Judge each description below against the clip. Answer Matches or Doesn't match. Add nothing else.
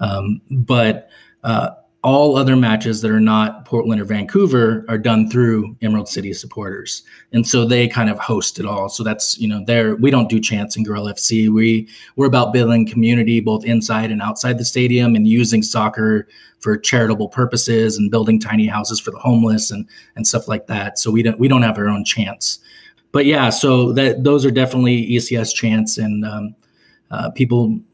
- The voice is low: Matches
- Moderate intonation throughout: Doesn't match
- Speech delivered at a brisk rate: Doesn't match